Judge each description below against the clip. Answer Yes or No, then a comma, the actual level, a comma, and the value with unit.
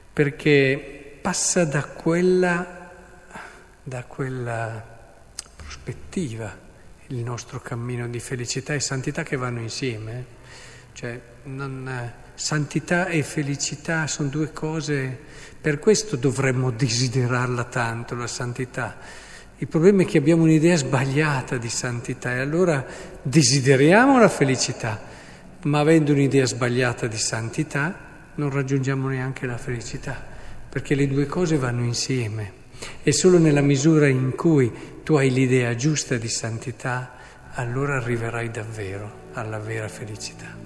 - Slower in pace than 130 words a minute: Yes, average, 120 wpm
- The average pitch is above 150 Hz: No, low, 135 Hz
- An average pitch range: Yes, average, 3.6 semitones